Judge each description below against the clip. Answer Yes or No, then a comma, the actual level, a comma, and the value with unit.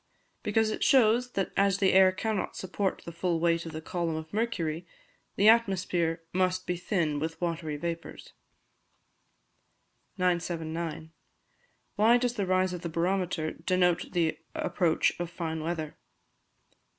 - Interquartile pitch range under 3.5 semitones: Yes, average, 3.0 semitones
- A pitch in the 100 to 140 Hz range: No, medium, 175 Hz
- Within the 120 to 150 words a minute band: Yes, average, 140 wpm